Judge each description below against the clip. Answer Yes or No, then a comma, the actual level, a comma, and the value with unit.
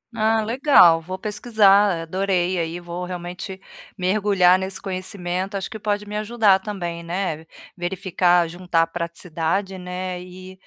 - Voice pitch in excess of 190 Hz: No, medium, 185 Hz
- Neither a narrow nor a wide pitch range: No, narrow, 2.2 semitones